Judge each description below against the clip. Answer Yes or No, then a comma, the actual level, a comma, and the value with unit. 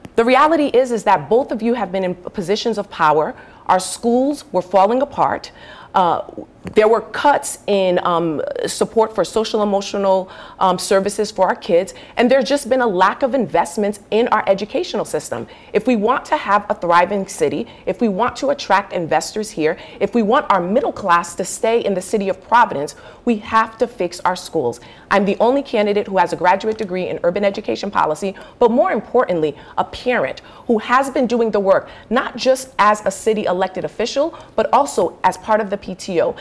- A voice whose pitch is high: Yes, high, 210 Hz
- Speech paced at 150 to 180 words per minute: No, average, 195 wpm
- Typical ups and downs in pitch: Yes, average, 4.1 semitones